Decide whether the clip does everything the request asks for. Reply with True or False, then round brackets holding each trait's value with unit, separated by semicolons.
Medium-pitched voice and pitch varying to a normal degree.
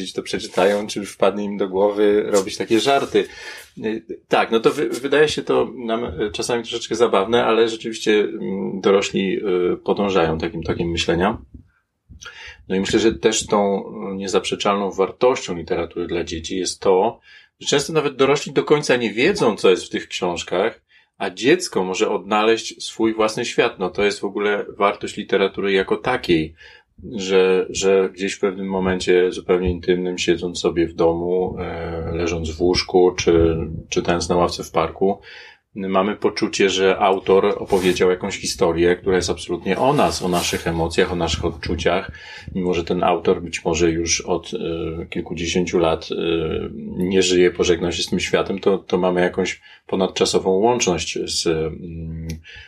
False (95 Hz; 4.4 semitones)